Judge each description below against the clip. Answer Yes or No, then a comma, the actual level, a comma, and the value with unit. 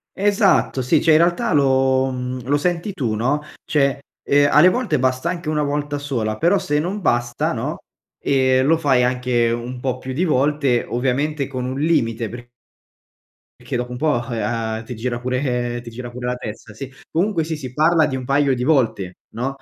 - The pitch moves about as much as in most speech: Yes, average, 3.5 semitones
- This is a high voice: No, low, 130 Hz